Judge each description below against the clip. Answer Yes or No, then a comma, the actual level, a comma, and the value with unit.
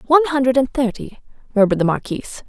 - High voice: Yes, high, 245 Hz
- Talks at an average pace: Yes, average, 170 wpm